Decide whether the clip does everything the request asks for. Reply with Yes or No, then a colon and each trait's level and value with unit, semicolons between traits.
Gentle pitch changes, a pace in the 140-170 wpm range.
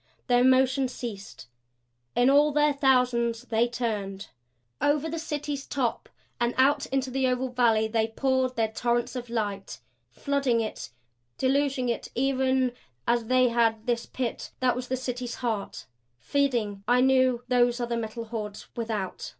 Yes: narrow, 2.3 semitones; average, 150 wpm